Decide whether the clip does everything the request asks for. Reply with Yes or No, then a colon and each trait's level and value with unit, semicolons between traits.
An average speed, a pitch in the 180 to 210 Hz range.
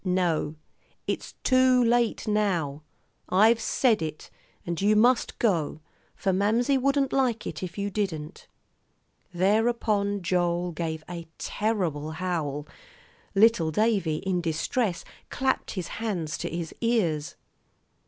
No: slow, 120 wpm; high, 190 Hz